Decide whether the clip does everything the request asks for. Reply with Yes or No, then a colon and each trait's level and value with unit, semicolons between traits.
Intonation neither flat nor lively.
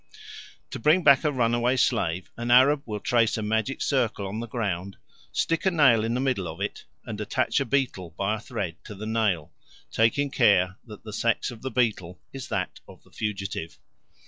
Yes: average, 4.3 semitones